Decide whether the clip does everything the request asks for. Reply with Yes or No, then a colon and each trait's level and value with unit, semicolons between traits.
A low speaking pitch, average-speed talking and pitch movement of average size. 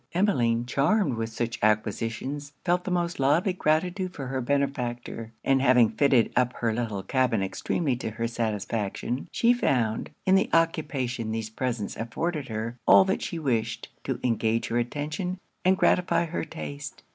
No: low, 125 Hz; average, 155 wpm; wide, 5.7 semitones